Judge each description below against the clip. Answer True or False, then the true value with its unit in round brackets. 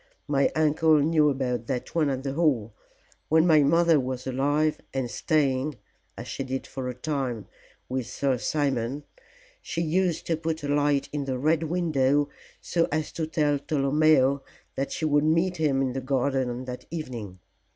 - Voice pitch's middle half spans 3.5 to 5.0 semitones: False (3.0 semitones)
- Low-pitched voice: False (145 Hz)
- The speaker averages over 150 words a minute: True (170 wpm)